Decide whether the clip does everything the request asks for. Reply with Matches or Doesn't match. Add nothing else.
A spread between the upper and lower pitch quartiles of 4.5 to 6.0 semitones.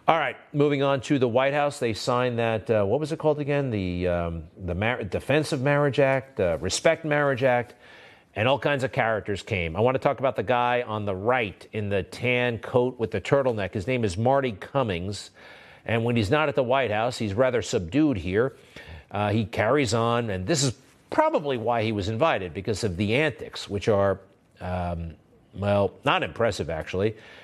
Matches